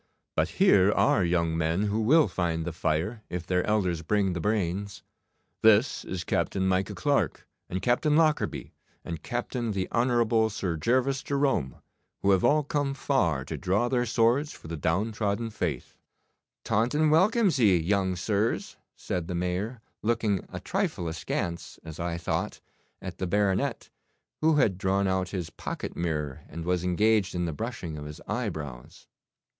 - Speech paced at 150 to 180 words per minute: Yes, average, 160 wpm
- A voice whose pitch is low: Yes, very low, 95 Hz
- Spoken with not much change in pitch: No, average, 5.3 semitones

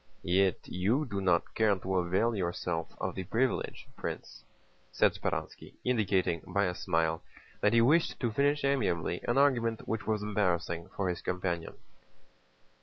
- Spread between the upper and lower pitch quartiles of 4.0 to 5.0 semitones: Yes, average, 4.7 semitones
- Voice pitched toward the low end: Yes, low, 100 Hz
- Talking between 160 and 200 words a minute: No, average, 150 wpm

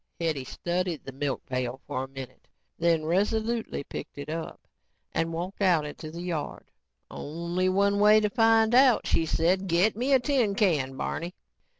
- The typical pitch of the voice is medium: Yes, medium, 175 Hz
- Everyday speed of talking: Yes, average, 175 wpm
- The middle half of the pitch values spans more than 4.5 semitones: Yes, average, 5.2 semitones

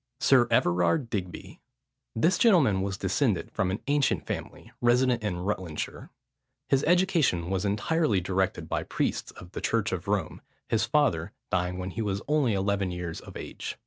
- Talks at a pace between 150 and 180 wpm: Yes, average, 160 wpm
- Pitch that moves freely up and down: Yes, wide, 5.8 semitones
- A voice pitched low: Yes, low, 100 Hz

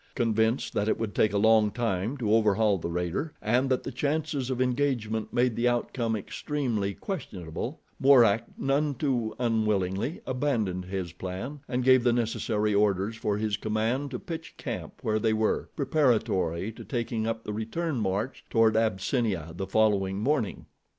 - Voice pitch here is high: No, low, 110 Hz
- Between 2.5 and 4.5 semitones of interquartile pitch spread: Yes, average, 3.7 semitones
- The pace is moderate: Yes, average, 160 wpm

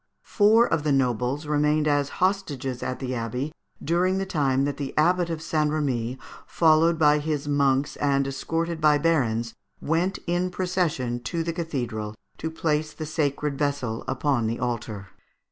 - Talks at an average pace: Yes, average, 160 wpm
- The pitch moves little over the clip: No, average, 3.9 semitones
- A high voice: No, medium, 150 Hz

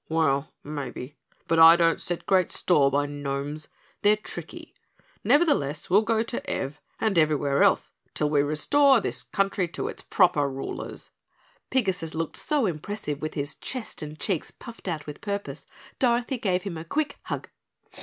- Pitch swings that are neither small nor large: No, wide, 6.0 semitones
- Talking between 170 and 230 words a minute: No, average, 160 wpm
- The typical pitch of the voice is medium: Yes, medium, 165 Hz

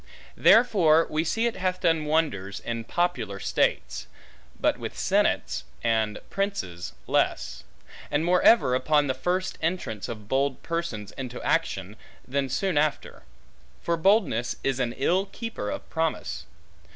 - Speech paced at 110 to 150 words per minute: Yes, average, 140 wpm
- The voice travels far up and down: Yes, wide, 7.2 semitones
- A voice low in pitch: No, medium, 150 Hz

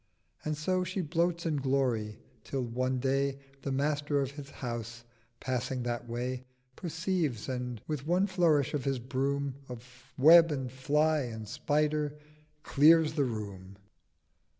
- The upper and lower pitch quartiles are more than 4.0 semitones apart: No, average, 3.6 semitones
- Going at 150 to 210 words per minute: No, average, 140 wpm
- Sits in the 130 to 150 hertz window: Yes, low, 135 Hz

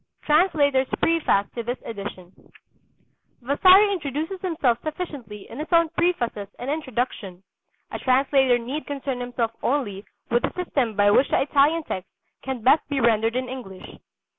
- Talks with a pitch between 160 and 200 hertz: No, very high, 265 Hz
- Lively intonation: No, average, 4.9 semitones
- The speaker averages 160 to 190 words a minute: No, average, 145 wpm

